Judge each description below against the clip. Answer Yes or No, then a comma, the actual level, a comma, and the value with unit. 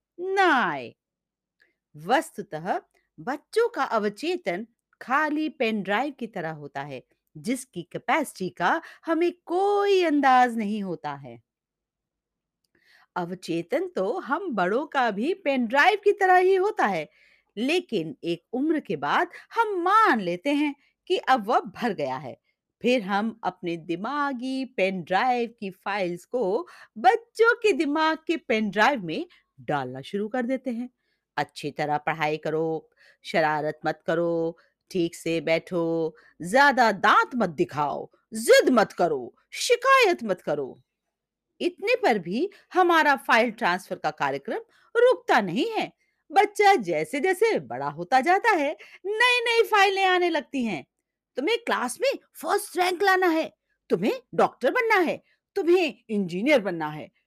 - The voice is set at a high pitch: Yes, very high, 260 Hz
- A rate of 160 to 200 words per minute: No, average, 135 wpm